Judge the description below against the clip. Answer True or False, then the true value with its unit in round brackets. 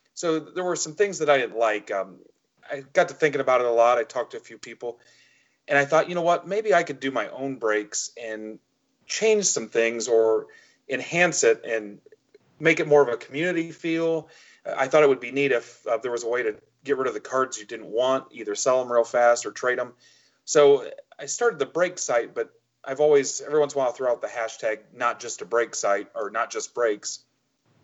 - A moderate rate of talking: False (235 wpm)